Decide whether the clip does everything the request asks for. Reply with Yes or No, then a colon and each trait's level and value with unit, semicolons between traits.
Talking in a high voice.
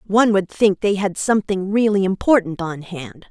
Yes: high, 195 Hz